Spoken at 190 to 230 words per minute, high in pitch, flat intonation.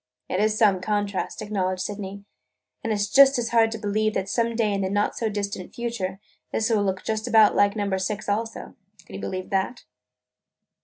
Yes: average, 200 wpm; high, 205 Hz; narrow, 2.2 semitones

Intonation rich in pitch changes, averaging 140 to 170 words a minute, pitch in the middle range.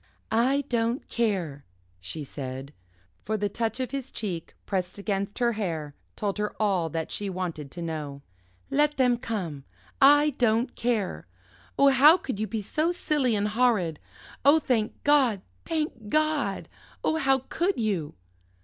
No: wide, 6.6 semitones; average, 150 wpm; high, 220 Hz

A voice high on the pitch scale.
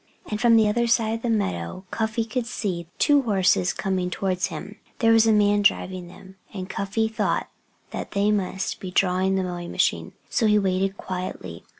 Yes: high, 200 Hz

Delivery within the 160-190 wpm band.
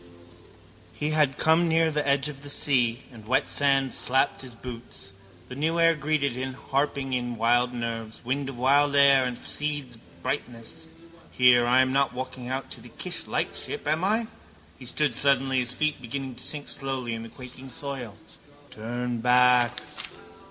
Yes: average, 175 wpm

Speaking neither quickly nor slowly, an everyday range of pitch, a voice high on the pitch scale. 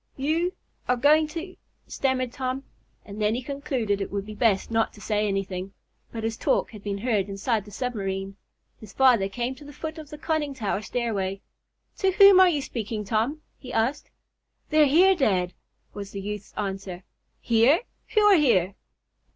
No: average, 180 wpm; wide, 6.2 semitones; high, 230 Hz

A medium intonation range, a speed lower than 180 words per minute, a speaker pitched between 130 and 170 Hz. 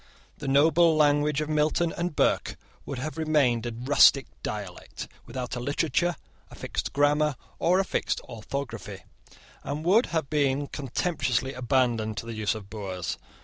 Yes: average, 4.1 semitones; average, 150 wpm; medium, 140 Hz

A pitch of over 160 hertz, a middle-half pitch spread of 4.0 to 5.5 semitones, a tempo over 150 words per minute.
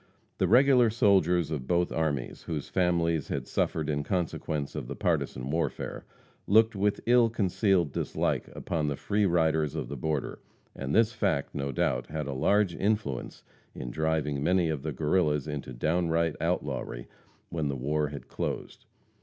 No: very low, 80 Hz; average, 4.6 semitones; average, 160 wpm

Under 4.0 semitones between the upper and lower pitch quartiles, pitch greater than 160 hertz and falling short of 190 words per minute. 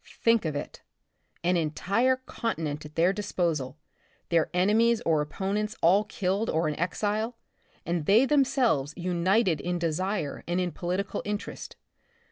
No: average, 4.4 semitones; medium, 185 Hz; slow, 135 wpm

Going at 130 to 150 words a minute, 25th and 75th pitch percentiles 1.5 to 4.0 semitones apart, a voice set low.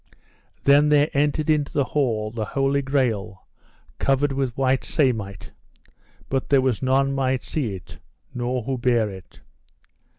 Yes: average, 140 wpm; average, 3.0 semitones; low, 130 Hz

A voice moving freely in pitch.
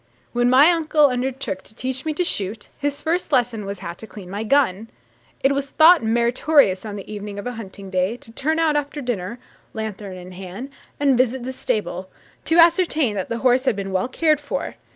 Yes: wide, 5.9 semitones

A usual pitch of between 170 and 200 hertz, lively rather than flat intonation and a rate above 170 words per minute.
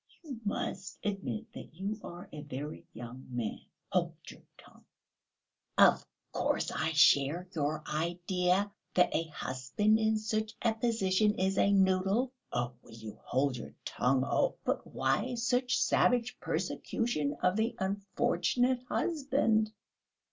No: high, 190 Hz; wide, 6.7 semitones; slow, 135 wpm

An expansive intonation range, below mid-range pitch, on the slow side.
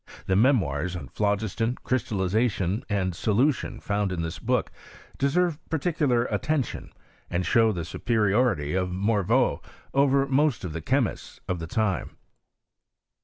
Yes: wide, 5.7 semitones; low, 105 Hz; slow, 125 wpm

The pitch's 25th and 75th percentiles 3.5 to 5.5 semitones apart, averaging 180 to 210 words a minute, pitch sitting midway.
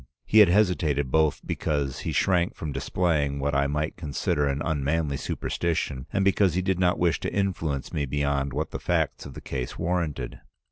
No: average, 3.8 semitones; average, 185 wpm; very low, 75 Hz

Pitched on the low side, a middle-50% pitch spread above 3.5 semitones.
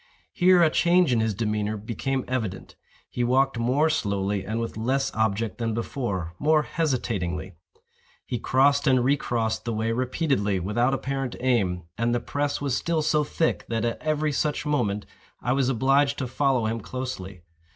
Yes: low, 125 Hz; average, 4.2 semitones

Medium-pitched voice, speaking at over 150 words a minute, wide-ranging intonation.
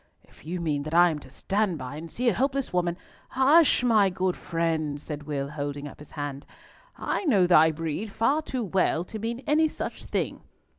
Yes: medium, 175 Hz; average, 200 wpm; wide, 7.1 semitones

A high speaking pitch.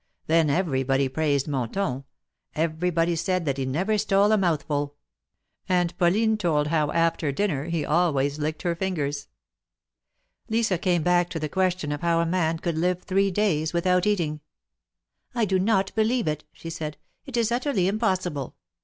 No: medium, 170 Hz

